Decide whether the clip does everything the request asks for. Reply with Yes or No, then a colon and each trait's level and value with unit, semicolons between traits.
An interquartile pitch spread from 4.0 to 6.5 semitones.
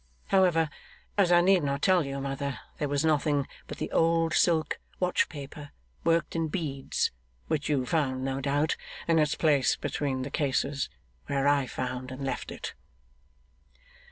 No: average, 3.1 semitones